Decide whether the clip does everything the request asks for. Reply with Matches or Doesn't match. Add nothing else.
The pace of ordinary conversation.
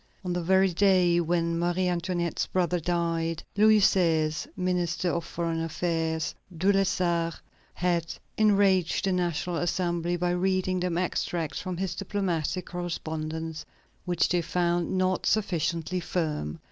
Doesn't match